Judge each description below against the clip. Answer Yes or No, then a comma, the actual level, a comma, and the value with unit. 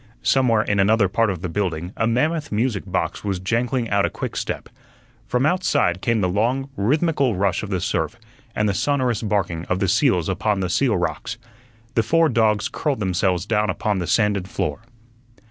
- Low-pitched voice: Yes, low, 105 Hz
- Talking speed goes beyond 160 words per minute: Yes, average, 180 wpm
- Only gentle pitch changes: No, average, 4.5 semitones